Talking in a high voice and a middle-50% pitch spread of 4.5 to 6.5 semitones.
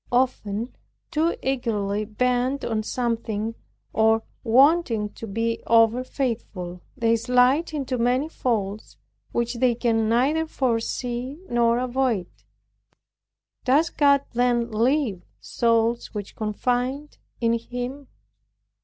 No: high, 240 Hz; narrow, 2.5 semitones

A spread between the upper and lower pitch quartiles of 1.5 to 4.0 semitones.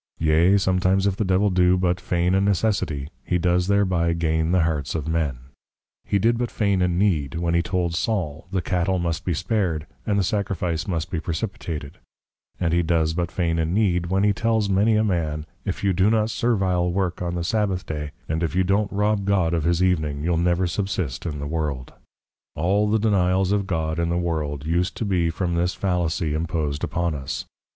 Yes: average, 2.9 semitones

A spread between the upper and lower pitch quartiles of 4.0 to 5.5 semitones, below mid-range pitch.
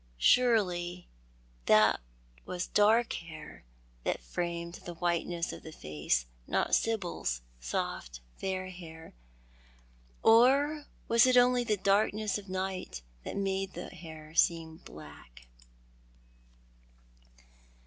No: average, 4.7 semitones; medium, 180 Hz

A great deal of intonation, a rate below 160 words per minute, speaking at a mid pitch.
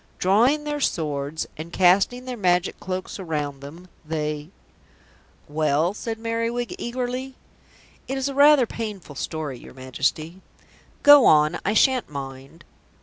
Yes: wide, 8.2 semitones; slow, 135 wpm; medium, 180 Hz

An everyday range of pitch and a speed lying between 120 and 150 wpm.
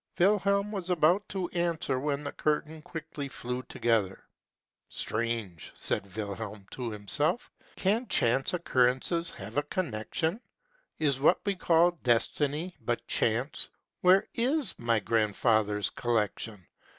No: wide, 7.4 semitones; average, 140 wpm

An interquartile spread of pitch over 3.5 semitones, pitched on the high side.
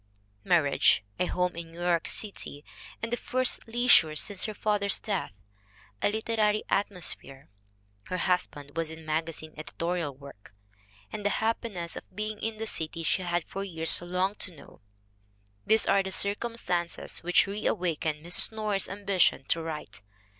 No: average, 4.2 semitones; medium, 180 Hz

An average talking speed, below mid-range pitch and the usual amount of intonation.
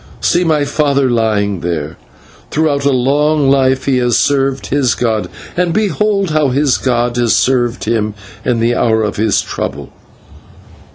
Yes: average, 155 wpm; low, 130 Hz; average, 3.8 semitones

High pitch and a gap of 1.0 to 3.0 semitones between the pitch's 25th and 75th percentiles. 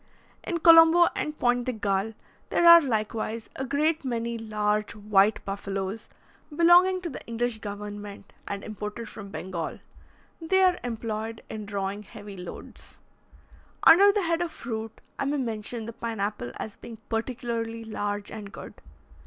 No: high, 225 Hz; average, 4.6 semitones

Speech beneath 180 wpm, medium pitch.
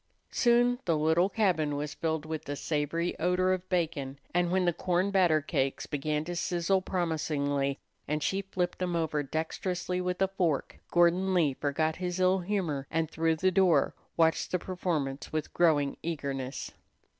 Yes: average, 160 wpm; medium, 170 Hz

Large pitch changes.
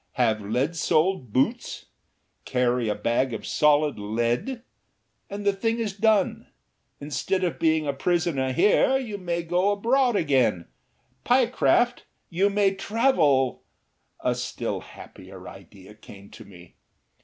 Yes: wide, 8.5 semitones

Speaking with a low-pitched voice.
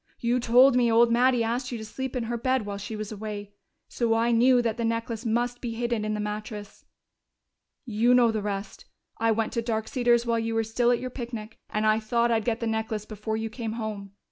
No: high, 230 Hz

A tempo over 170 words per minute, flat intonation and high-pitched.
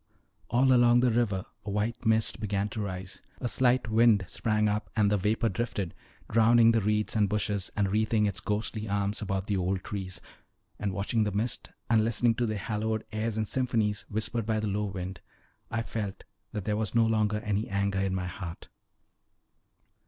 No: average, 185 wpm; narrow, 2.1 semitones; low, 105 Hz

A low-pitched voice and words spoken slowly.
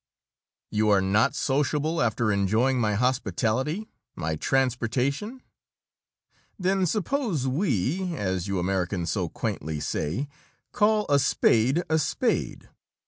Yes: low, 130 Hz; slow, 110 wpm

